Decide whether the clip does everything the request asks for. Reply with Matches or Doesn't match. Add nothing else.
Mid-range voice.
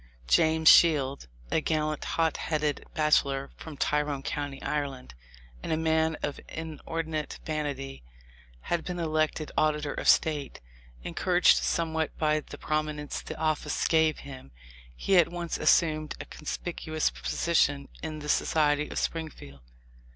Matches